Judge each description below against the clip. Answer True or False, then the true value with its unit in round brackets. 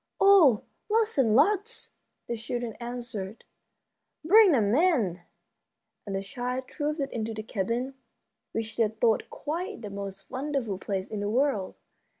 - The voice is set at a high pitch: True (240 Hz)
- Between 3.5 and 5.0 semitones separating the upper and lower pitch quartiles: False (5.6 semitones)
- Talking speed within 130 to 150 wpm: True (140 wpm)